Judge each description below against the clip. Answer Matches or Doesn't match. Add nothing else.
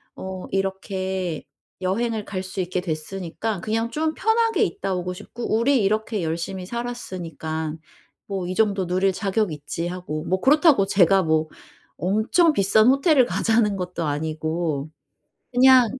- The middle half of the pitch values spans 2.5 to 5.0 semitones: Matches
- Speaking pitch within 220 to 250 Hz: Doesn't match